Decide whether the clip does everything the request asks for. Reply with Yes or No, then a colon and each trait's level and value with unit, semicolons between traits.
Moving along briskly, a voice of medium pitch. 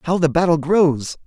No: average, 190 wpm; medium, 160 Hz